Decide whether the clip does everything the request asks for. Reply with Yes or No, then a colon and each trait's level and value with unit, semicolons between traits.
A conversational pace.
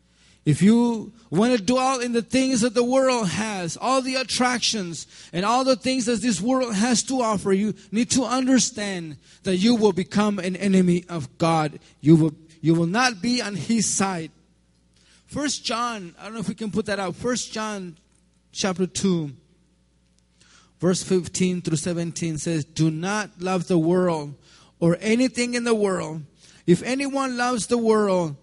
Yes: average, 170 wpm